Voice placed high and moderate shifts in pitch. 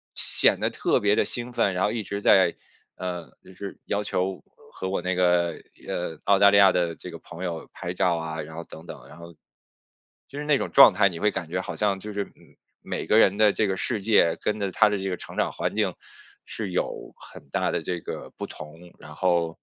No: very low, 95 Hz; average, 3.0 semitones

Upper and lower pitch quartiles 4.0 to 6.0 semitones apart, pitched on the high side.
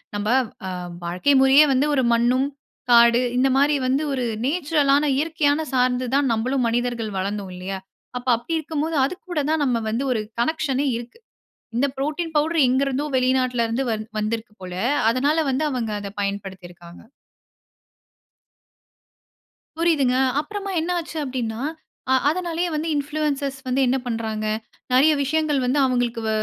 Yes: average, 4.3 semitones; very high, 260 Hz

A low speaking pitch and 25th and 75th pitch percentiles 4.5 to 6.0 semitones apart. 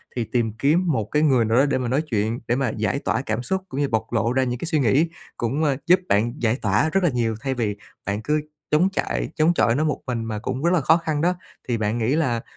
Yes: low, 125 Hz; average, 5.2 semitones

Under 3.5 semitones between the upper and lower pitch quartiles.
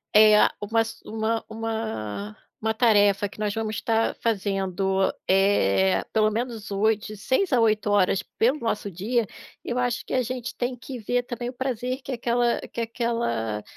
Yes: average, 2.9 semitones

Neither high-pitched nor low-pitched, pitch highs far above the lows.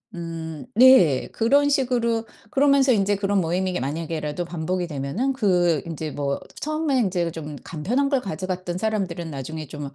Yes: medium, 180 Hz; wide, 6.7 semitones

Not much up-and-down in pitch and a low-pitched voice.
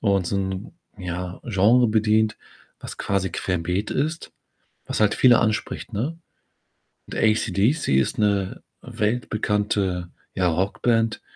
No: average, 3.1 semitones; low, 105 Hz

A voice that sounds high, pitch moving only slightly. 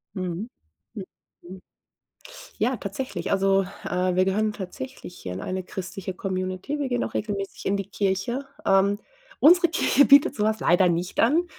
No: high, 195 Hz; average, 3.5 semitones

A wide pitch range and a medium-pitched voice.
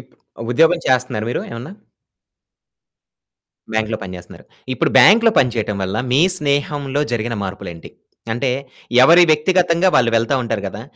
No: wide, 5.7 semitones; low, 125 Hz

